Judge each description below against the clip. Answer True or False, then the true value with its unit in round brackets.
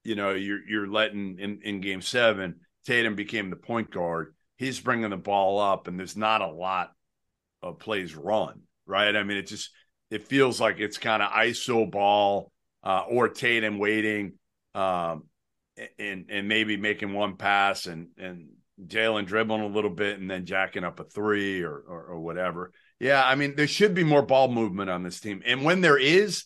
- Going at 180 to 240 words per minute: True (190 wpm)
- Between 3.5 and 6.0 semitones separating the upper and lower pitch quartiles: False (2.5 semitones)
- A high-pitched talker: False (105 Hz)